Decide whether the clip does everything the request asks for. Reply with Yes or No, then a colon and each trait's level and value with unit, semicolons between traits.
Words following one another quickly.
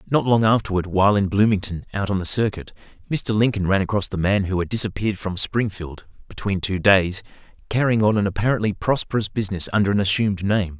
No: average, 190 wpm